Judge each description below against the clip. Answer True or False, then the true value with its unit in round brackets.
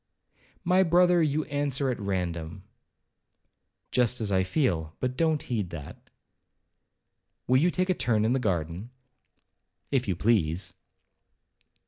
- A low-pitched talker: True (120 Hz)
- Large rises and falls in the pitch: True (7.9 semitones)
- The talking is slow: True (120 wpm)